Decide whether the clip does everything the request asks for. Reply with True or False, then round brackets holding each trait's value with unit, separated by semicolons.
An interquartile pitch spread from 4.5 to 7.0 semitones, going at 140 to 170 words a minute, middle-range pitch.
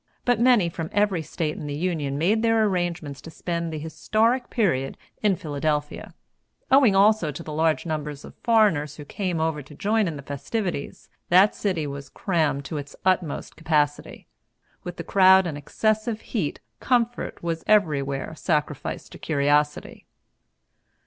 True (5.6 semitones; 155 wpm; 165 Hz)